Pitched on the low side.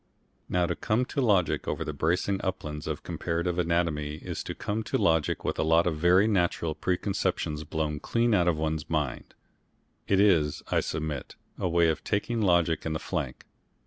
Yes: very low, 85 Hz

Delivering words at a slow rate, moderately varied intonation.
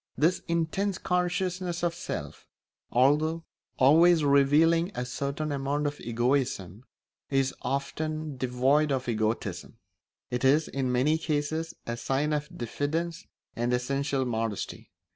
Yes: slow, 120 wpm; average, 4.1 semitones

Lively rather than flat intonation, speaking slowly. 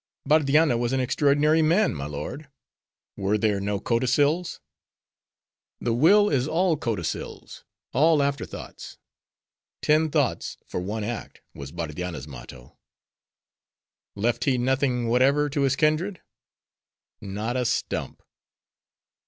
Yes: wide, 6.3 semitones; slow, 115 wpm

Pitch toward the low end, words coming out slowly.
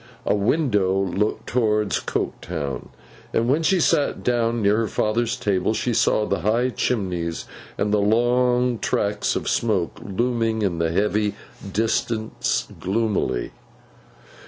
Yes: low, 110 Hz; slow, 130 wpm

